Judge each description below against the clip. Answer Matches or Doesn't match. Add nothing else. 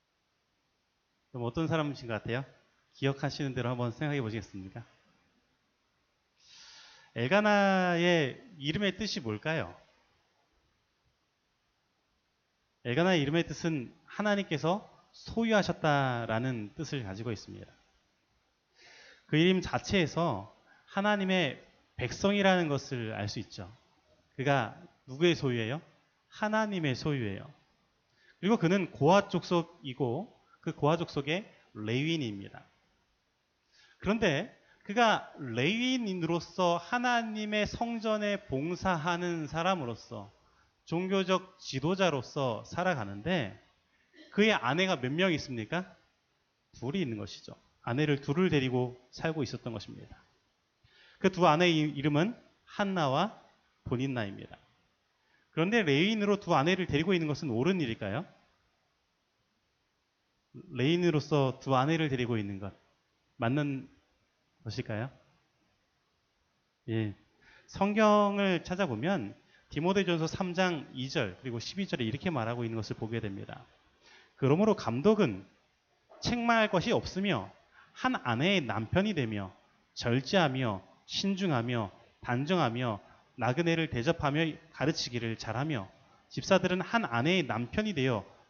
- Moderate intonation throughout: Doesn't match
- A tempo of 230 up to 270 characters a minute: Matches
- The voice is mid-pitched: Matches